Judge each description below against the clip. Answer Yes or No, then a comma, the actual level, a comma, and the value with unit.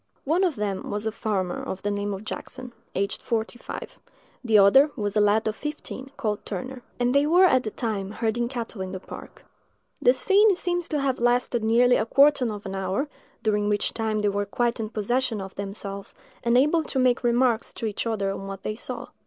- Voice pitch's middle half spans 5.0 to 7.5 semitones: No, average, 4.0 semitones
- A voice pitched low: No, high, 225 Hz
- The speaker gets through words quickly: Yes, fast, 210 wpm